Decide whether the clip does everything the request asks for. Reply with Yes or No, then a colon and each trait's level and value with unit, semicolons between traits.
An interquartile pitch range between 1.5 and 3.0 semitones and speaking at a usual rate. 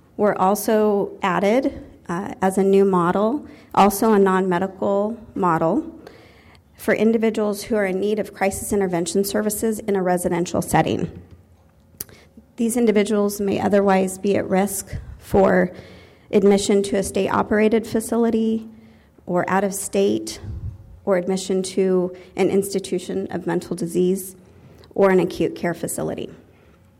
No: narrow, 2.6 semitones; slow, 125 wpm